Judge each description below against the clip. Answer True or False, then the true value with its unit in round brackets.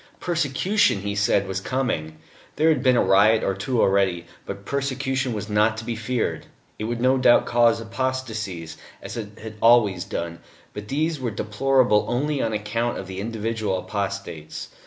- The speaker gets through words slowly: False (170 wpm)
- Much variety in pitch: False (4.5 semitones)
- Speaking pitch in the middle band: False (110 Hz)